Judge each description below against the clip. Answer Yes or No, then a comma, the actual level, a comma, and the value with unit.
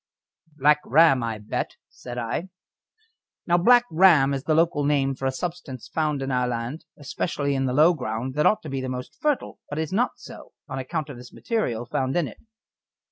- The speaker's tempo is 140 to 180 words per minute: No, average, 200 wpm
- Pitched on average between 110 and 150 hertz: Yes, medium, 140 Hz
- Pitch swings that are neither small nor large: Yes, average, 4.0 semitones